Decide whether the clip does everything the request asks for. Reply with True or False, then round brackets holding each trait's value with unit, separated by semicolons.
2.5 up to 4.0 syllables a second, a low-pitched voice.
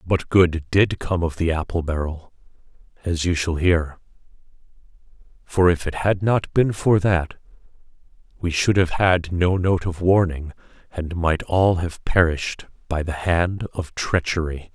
False (4.2 syllables/s; 85 Hz)